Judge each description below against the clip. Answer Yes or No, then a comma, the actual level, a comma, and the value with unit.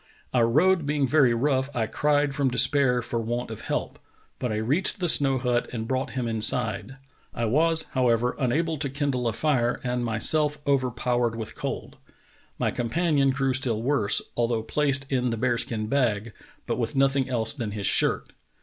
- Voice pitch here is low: Yes, low, 125 Hz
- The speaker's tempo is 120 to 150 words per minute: No, average, 180 wpm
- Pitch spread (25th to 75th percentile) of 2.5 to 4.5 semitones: Yes, average, 3.3 semitones